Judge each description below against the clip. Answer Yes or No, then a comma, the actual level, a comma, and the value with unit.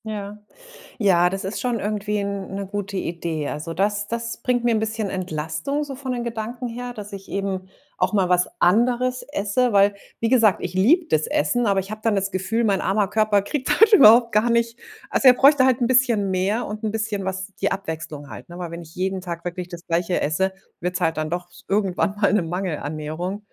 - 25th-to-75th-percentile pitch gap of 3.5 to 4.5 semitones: Yes, average, 4.2 semitones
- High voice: Yes, high, 200 Hz